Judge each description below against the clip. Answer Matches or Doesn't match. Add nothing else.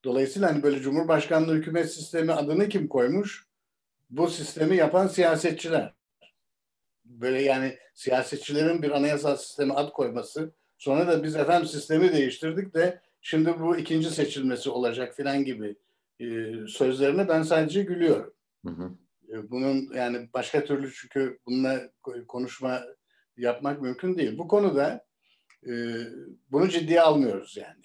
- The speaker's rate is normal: Matches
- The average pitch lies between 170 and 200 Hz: Doesn't match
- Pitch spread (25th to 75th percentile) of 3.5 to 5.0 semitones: Matches